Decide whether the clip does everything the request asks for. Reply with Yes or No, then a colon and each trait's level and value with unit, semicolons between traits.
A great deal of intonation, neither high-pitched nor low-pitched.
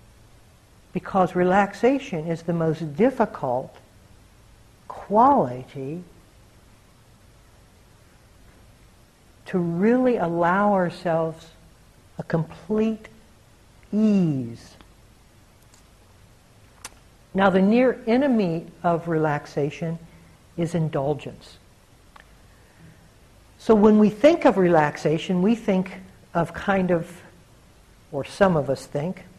Yes: wide, 8.4 semitones; medium, 160 Hz